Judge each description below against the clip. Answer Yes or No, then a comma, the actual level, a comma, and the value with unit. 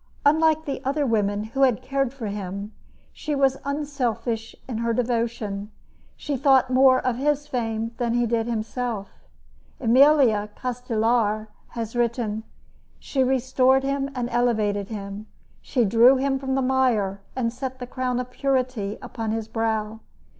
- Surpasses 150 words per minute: No, average, 145 wpm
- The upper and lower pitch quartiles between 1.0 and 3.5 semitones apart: Yes, average, 3.2 semitones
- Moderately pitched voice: No, high, 245 Hz